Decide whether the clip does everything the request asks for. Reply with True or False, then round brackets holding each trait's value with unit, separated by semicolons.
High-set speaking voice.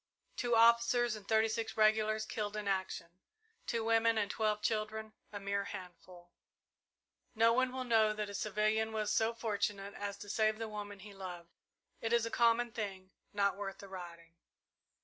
True (215 Hz)